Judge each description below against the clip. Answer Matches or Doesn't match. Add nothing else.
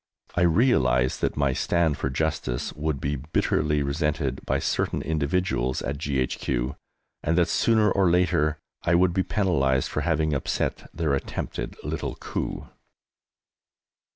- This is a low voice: Matches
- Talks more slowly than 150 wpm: Matches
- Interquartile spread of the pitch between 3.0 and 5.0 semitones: Matches